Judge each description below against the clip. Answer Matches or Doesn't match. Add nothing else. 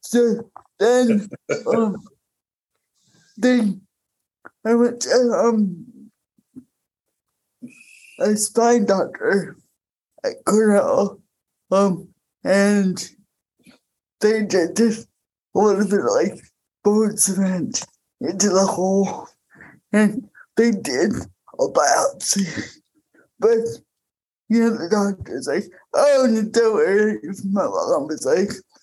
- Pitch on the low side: Doesn't match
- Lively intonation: Doesn't match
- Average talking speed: Doesn't match